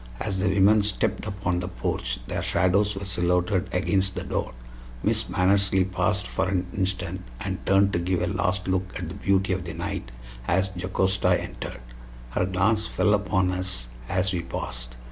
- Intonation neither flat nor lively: No, narrow, 1.4 semitones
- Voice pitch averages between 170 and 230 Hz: No, very low, 95 Hz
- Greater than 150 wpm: Yes, average, 175 wpm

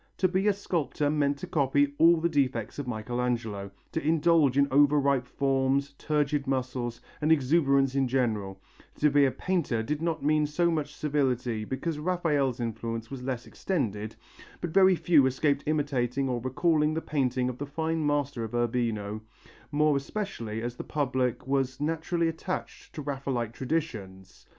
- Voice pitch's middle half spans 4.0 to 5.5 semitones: No, average, 3.6 semitones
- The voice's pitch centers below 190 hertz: Yes, medium, 140 Hz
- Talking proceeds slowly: No, average, 160 wpm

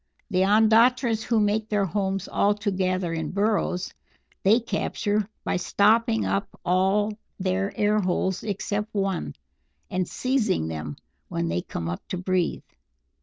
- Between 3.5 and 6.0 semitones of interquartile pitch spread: No, narrow, 2.6 semitones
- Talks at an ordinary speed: No, slow, 130 wpm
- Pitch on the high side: Yes, high, 200 Hz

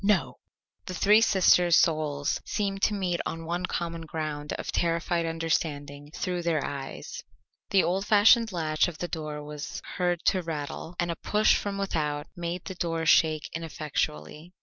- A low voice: No, medium, 170 Hz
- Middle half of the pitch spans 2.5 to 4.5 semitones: Yes, average, 2.9 semitones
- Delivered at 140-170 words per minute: Yes, average, 160 wpm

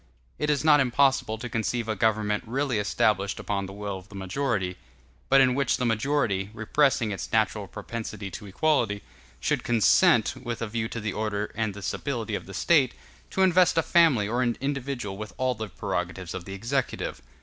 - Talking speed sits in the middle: Yes, average, 190 wpm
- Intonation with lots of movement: No, average, 4.6 semitones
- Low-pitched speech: Yes, low, 110 Hz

